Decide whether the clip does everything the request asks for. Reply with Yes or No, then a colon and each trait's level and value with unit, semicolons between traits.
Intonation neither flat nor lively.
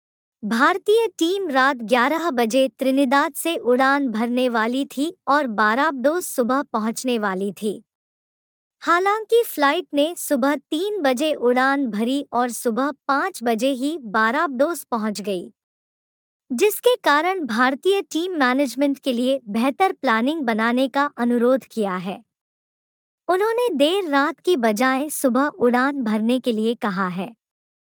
Yes: average, 4.3 semitones